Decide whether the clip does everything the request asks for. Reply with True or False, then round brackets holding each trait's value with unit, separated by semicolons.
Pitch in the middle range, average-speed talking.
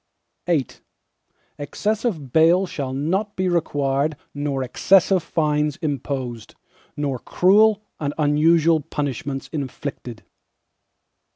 False (150 Hz; 90 wpm)